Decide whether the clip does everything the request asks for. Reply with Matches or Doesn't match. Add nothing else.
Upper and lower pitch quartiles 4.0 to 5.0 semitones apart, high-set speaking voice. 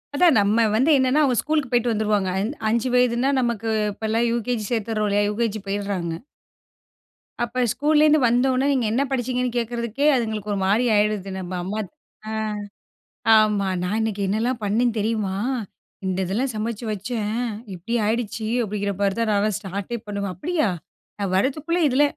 Doesn't match